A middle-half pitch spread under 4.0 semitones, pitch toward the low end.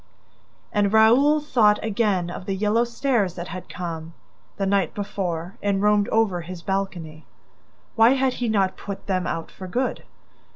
No: average, 3.6 semitones; high, 200 Hz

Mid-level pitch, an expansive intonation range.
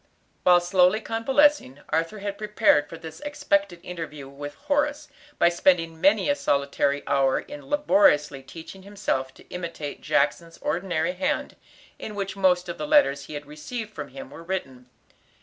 Yes: medium, 180 Hz; wide, 6.4 semitones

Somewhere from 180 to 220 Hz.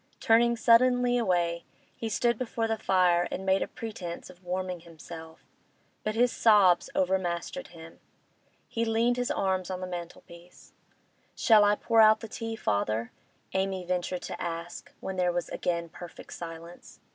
Yes: medium, 185 Hz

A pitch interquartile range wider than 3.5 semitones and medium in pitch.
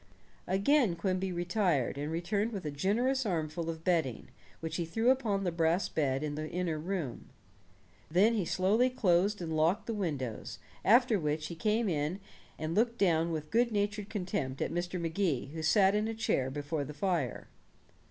Yes: average, 4.7 semitones; medium, 175 Hz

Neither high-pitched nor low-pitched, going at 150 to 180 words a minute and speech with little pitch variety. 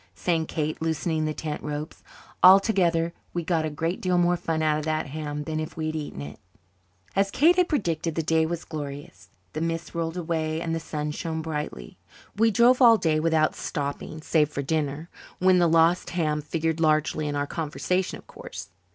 No: medium, 160 Hz; average, 195 wpm; narrow, 1.9 semitones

